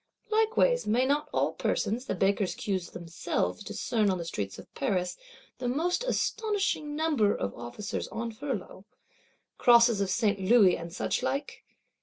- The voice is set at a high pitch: Yes, high, 225 Hz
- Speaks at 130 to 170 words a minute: Yes, average, 150 wpm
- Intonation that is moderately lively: No, wide, 7.3 semitones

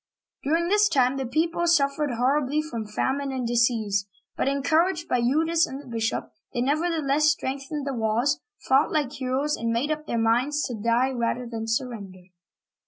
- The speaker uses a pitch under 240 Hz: No, very high, 265 Hz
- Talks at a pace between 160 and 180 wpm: Yes, average, 170 wpm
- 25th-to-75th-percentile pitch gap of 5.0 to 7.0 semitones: No, average, 4.2 semitones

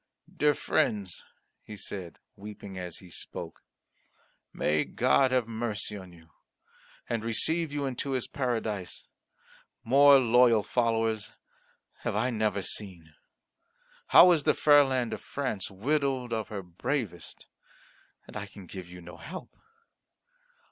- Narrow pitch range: No, average, 5.3 semitones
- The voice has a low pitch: Yes, low, 110 Hz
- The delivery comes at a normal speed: No, slow, 130 wpm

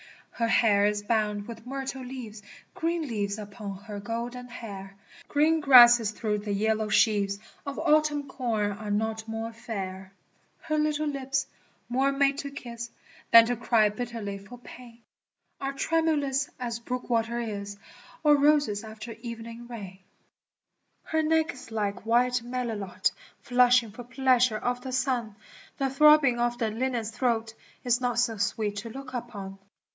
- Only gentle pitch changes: No, average, 3.4 semitones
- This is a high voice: Yes, high, 235 Hz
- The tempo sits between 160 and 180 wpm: No, average, 150 wpm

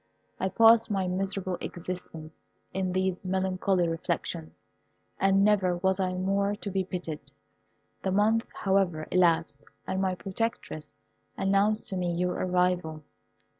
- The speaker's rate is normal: No, slow, 130 wpm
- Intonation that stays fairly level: Yes, narrow, 1.6 semitones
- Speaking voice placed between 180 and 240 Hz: Yes, medium, 185 Hz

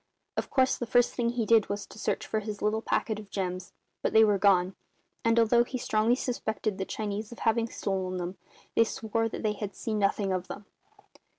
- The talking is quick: Yes, fast, 210 wpm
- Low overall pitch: No, high, 215 Hz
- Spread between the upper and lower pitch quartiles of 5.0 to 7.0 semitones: No, narrow, 2.4 semitones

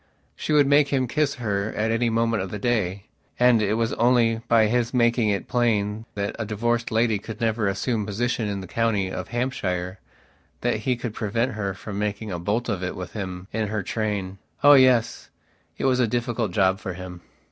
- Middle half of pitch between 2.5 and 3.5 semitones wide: Yes, average, 3.2 semitones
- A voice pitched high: No, low, 110 Hz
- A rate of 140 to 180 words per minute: No, fast, 205 wpm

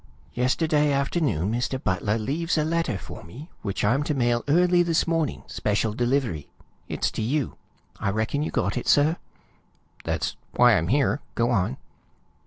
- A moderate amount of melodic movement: No, wide, 5.8 semitones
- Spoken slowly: No, average, 160 wpm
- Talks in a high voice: No, low, 130 Hz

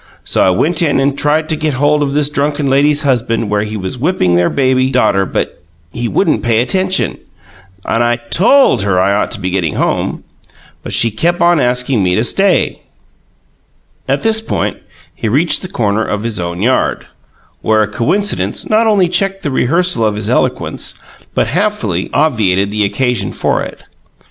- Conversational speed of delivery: Yes, average, 185 wpm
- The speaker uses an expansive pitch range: Yes, wide, 6.7 semitones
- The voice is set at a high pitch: No, low, 125 Hz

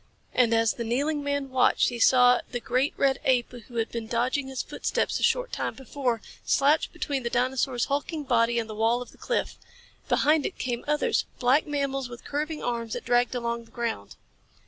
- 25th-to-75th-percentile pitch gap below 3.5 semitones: Yes, average, 2.9 semitones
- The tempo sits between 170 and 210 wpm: Yes, average, 195 wpm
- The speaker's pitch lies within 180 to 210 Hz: No, very high, 250 Hz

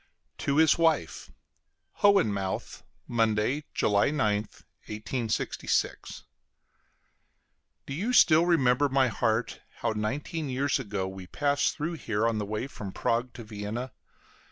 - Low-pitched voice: Yes, low, 120 Hz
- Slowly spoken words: Yes, slow, 120 wpm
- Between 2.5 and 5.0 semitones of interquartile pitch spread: No, wide, 5.4 semitones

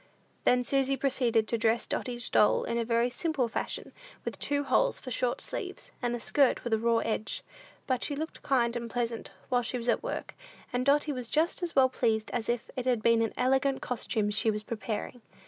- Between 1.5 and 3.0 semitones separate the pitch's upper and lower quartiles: Yes, narrow, 2.5 semitones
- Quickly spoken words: Yes, fast, 210 wpm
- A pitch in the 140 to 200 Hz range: No, high, 245 Hz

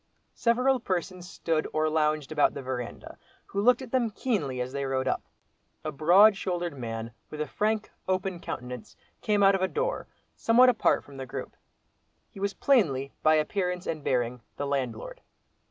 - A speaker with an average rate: Yes, average, 170 wpm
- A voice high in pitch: No, medium, 165 Hz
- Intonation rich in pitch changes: Yes, wide, 6.9 semitones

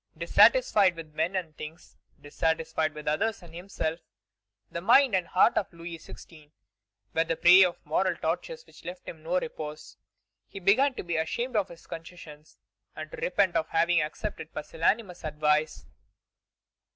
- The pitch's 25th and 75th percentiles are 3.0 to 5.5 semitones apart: Yes, average, 3.4 semitones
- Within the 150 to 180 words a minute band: Yes, average, 155 wpm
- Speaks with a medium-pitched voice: Yes, medium, 170 Hz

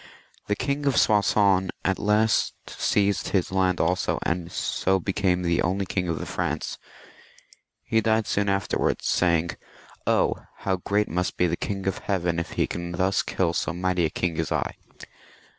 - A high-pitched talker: No, very low, 95 Hz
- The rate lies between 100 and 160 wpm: No, average, 175 wpm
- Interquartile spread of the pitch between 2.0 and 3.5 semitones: Yes, narrow, 2.5 semitones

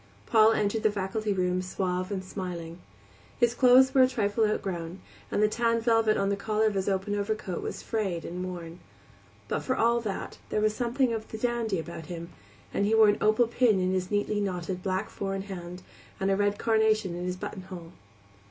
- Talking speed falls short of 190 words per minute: No, average, 200 wpm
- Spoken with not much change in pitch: No, average, 3.2 semitones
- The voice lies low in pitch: No, high, 205 Hz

